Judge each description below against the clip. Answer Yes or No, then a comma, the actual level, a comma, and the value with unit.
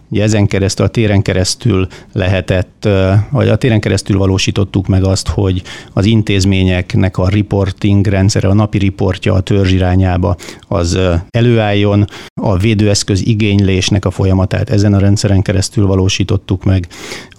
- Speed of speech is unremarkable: Yes, average, 135 wpm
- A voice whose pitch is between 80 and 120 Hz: Yes, low, 100 Hz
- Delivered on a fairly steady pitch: Yes, narrow, 2.0 semitones